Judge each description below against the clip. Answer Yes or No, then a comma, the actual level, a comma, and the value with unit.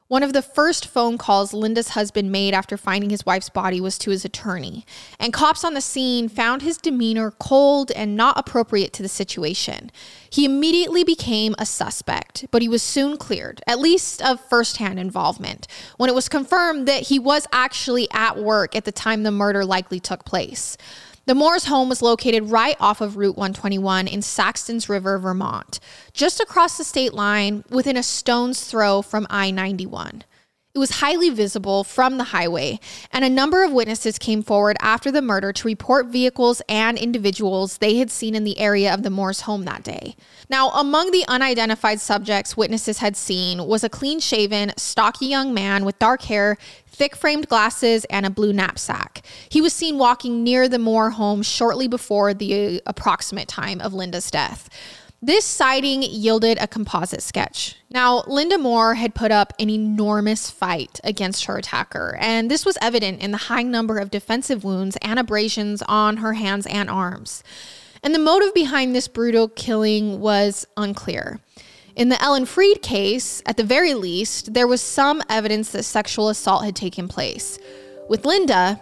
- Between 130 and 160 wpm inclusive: No, average, 175 wpm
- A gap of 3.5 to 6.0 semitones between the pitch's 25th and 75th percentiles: Yes, average, 4.0 semitones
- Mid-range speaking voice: No, high, 225 Hz